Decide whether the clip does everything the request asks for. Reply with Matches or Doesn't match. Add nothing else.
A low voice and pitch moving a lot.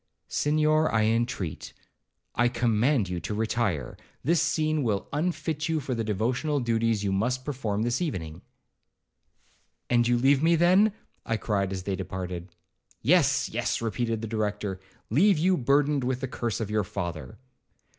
Matches